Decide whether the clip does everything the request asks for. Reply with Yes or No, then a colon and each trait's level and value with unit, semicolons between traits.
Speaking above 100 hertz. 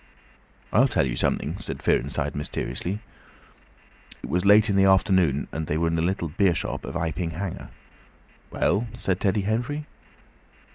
No: very low, 95 Hz